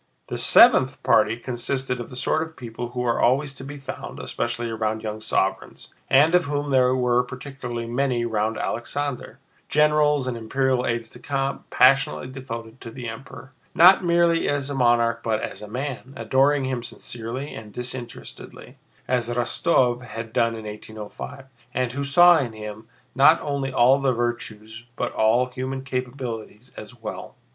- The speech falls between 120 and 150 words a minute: No, average, 160 wpm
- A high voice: No, low, 125 Hz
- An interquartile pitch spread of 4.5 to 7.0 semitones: No, average, 2.8 semitones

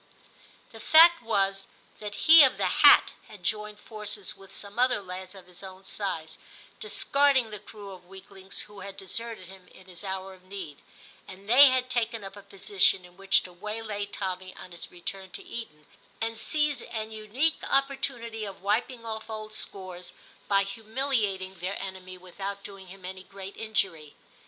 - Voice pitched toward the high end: Yes, high, 200 Hz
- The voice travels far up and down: No, average, 3.0 semitones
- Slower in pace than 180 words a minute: Yes, average, 170 wpm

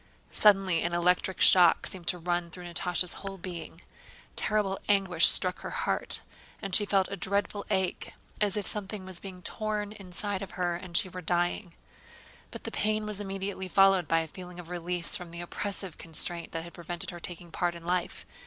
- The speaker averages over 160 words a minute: Yes, average, 180 wpm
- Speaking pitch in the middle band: Yes, medium, 180 Hz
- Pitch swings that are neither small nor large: No, narrow, 2.2 semitones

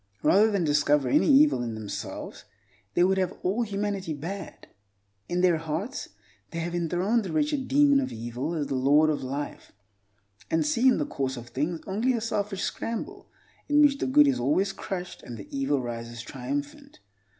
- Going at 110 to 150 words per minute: No, average, 180 wpm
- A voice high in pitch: No, medium, 175 Hz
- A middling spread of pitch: No, wide, 7.8 semitones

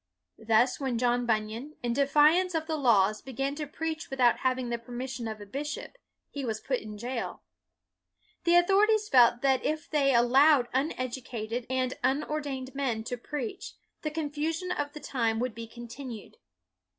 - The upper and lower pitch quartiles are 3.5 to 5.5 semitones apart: Yes, average, 4.0 semitones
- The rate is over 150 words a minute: Yes, average, 165 wpm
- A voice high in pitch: Yes, very high, 260 Hz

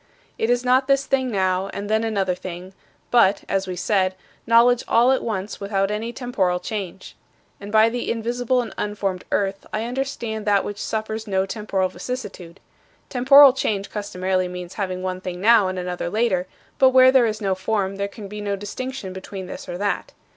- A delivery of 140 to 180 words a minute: No, average, 190 wpm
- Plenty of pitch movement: No, average, 3.8 semitones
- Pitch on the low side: No, high, 205 Hz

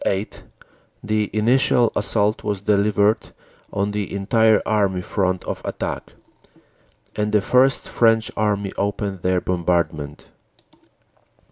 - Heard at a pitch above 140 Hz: No, low, 105 Hz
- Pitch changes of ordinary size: No, narrow, 2.0 semitones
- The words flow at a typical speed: No, slow, 110 wpm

